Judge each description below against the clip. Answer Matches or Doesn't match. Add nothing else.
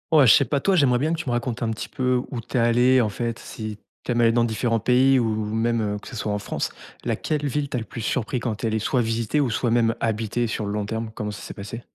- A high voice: Doesn't match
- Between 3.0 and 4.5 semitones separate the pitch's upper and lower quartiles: Doesn't match